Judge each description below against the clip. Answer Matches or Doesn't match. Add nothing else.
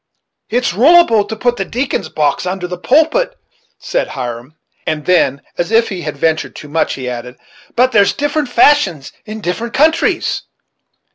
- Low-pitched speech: Doesn't match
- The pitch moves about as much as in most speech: Doesn't match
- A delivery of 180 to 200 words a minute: Doesn't match